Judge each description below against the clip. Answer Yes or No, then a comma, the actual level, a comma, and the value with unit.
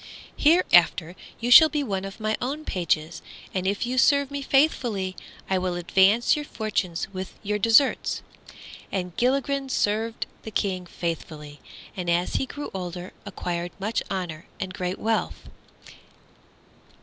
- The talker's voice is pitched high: Yes, high, 195 Hz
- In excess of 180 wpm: No, average, 145 wpm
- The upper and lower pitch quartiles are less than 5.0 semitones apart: No, wide, 5.6 semitones